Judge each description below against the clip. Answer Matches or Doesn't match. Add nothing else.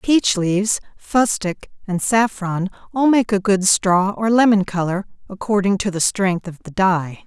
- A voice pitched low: Doesn't match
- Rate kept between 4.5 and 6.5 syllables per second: Doesn't match